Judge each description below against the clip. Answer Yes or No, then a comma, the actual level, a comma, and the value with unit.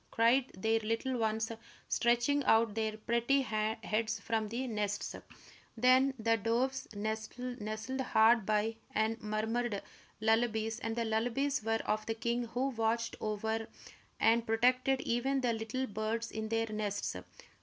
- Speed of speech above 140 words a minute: No, slow, 135 wpm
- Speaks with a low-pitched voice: No, high, 225 Hz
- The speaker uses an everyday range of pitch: No, narrow, 1.8 semitones